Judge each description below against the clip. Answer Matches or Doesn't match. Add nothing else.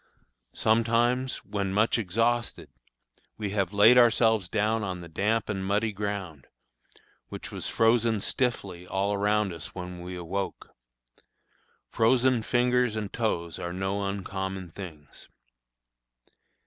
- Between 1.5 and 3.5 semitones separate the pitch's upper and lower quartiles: Matches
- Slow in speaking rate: Matches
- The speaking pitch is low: Matches